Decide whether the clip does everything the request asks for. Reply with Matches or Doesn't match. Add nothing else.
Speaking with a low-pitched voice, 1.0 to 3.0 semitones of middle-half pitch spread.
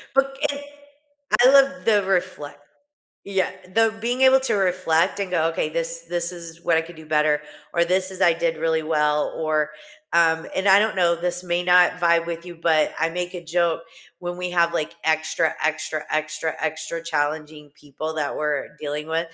Doesn't match